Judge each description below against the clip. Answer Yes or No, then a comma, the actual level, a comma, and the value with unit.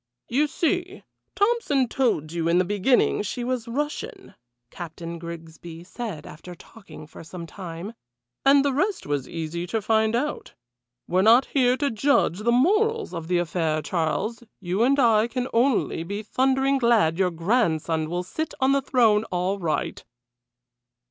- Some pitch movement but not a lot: No, wide, 7.6 semitones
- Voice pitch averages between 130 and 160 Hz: No, high, 215 Hz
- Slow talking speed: No, average, 155 wpm